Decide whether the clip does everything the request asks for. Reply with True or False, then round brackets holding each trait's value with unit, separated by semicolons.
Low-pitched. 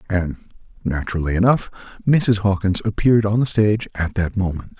True (100 Hz)